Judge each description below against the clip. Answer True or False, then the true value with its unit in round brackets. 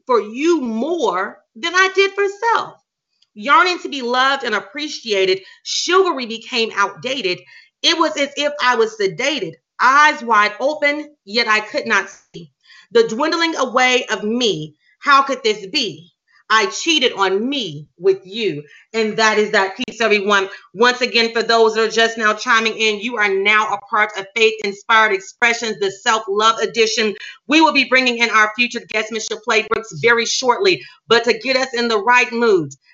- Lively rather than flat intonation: False (4.8 semitones)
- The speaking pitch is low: False (230 Hz)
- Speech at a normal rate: True (175 wpm)